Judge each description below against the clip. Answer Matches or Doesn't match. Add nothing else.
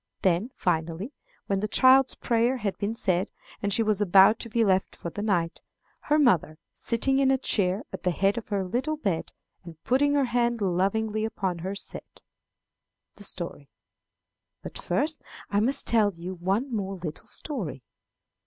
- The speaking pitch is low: Doesn't match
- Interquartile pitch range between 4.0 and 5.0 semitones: Matches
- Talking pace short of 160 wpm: Doesn't match